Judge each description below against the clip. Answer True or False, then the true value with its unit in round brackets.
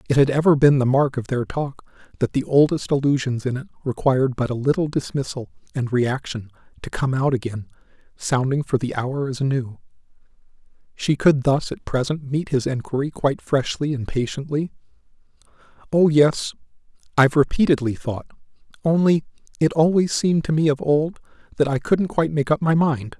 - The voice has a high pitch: False (140 Hz)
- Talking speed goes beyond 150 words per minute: True (170 wpm)